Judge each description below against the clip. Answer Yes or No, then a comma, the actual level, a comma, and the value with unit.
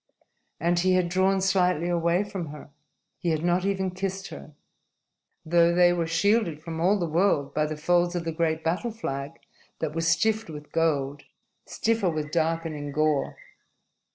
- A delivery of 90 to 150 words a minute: No, average, 165 wpm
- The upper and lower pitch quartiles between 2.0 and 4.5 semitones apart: Yes, average, 2.8 semitones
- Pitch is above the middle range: No, medium, 170 Hz